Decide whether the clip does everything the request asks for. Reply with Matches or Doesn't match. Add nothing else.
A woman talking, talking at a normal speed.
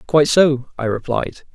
Doesn't match